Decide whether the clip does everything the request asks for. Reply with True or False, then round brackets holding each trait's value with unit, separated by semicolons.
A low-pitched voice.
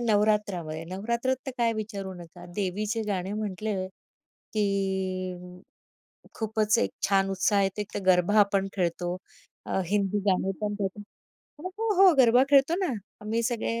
False (205 Hz)